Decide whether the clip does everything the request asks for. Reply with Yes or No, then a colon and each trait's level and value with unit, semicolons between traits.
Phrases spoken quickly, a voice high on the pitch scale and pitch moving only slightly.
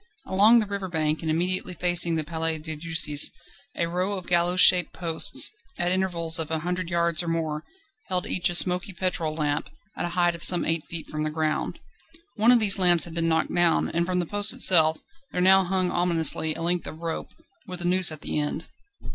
No: fast, 215 wpm; medium, 170 Hz; narrow, 2.1 semitones